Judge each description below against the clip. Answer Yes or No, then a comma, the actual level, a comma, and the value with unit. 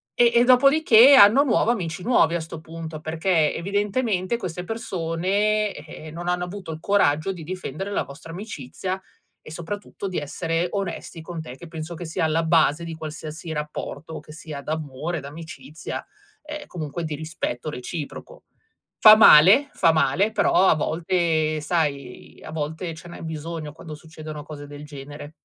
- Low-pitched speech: No, medium, 165 Hz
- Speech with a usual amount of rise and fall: Yes, average, 3.7 semitones